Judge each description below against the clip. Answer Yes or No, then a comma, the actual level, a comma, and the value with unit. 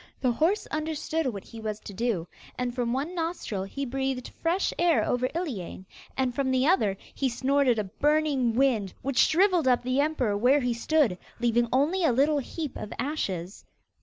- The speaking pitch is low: No, very high, 260 Hz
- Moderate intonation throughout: Yes, average, 4.7 semitones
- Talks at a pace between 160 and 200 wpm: Yes, average, 180 wpm